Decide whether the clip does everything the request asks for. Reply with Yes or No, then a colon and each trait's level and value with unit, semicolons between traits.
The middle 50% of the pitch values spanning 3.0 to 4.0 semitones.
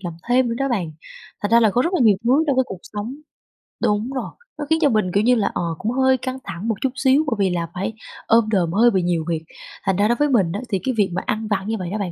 No: average, 5.1 semitones